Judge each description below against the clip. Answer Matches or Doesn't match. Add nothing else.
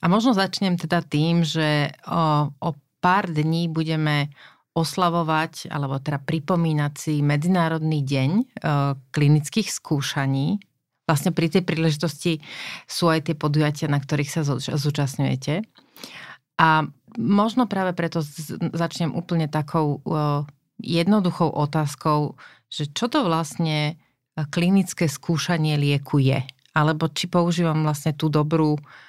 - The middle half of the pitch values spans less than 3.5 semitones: Matches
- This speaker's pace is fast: Doesn't match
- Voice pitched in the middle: Matches